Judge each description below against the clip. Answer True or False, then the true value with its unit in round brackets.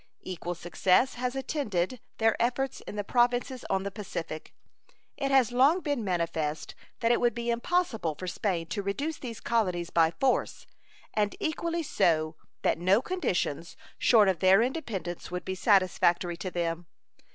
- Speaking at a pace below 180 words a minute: True (155 wpm)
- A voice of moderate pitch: False (205 Hz)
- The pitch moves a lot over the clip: True (6.0 semitones)